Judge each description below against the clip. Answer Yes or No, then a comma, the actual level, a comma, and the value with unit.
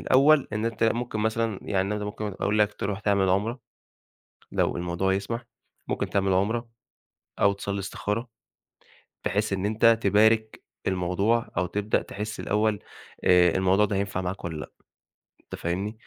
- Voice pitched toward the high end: No, low, 105 Hz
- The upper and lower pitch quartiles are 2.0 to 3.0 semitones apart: Yes, narrow, 2.4 semitones